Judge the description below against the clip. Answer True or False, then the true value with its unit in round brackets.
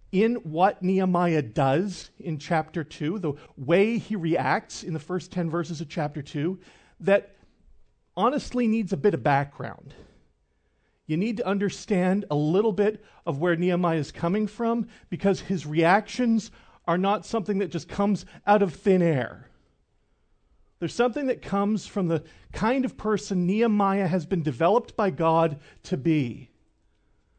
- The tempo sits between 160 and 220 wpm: False (150 wpm)